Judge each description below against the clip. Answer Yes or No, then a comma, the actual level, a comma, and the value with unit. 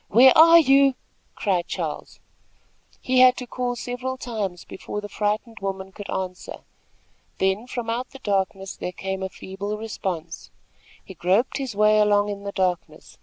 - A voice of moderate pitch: No, high, 210 Hz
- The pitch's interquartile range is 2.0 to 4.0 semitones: No, average, 4.4 semitones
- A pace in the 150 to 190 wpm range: Yes, average, 160 wpm